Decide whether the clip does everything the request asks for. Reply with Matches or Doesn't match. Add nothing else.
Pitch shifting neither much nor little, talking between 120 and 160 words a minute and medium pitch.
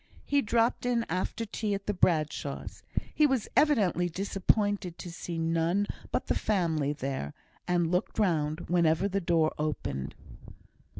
Matches